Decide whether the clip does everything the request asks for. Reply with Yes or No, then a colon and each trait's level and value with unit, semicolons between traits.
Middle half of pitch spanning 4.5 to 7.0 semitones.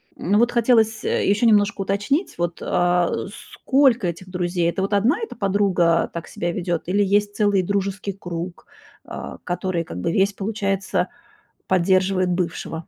No: average, 2.7 semitones